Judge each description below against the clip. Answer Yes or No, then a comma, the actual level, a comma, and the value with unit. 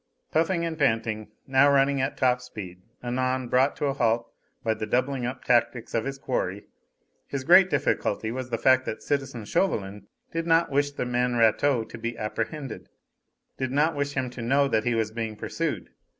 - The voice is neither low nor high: No, low, 125 Hz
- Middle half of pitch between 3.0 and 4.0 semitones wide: Yes, average, 3.6 semitones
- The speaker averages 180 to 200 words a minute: Yes, average, 185 wpm